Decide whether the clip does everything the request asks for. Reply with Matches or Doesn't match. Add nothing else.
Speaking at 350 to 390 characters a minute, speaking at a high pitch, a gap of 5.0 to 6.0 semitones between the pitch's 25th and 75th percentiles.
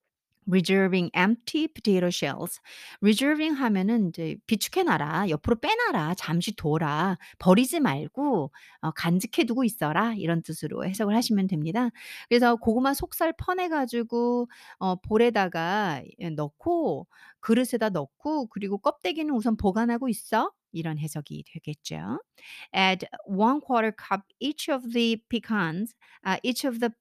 Matches